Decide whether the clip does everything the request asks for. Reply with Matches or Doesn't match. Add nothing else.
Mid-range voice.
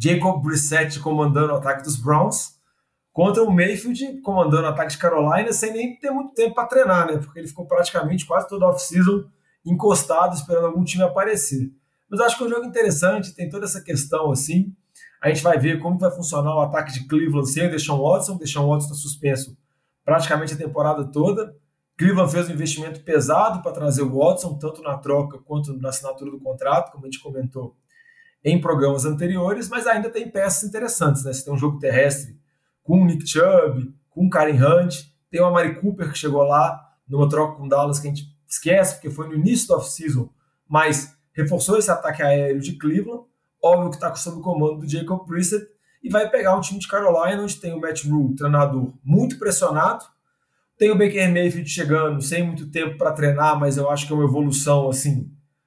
Matches